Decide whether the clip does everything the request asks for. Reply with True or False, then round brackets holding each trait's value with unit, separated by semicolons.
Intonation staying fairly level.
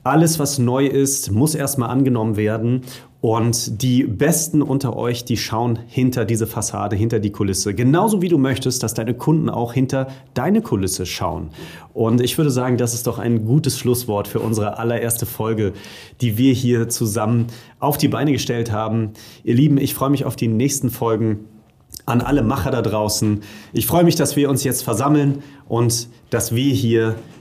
False (3.2 semitones)